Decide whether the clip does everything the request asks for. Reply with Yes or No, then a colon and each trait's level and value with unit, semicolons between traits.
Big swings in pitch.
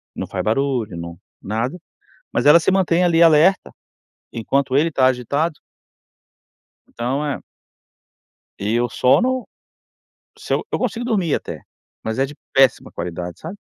Yes: wide, 6.3 semitones